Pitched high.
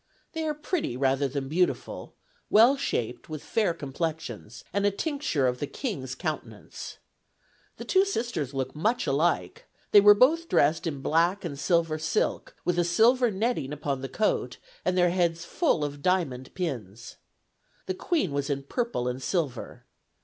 No: medium, 170 Hz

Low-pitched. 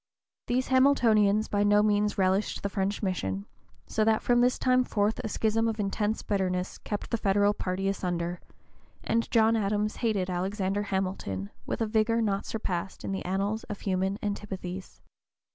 No: high, 205 Hz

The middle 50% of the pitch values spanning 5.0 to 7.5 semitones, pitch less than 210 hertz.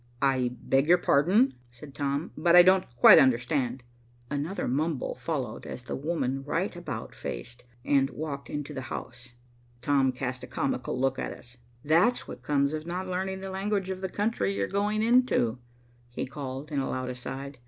Yes: wide, 5.5 semitones; medium, 140 Hz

